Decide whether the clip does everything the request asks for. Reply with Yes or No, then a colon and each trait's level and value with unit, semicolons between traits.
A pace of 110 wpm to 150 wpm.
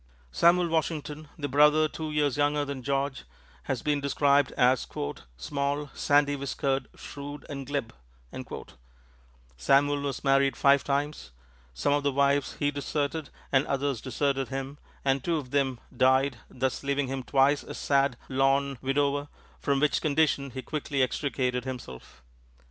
Yes: average, 145 wpm